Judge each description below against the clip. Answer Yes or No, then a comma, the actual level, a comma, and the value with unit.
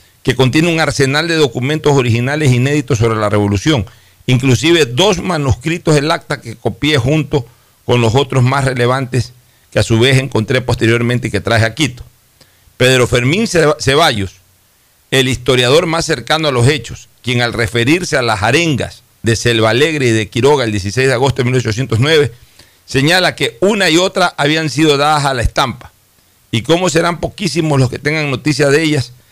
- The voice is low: Yes, low, 130 Hz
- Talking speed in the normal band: Yes, average, 170 wpm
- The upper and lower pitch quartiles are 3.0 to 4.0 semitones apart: No, average, 4.5 semitones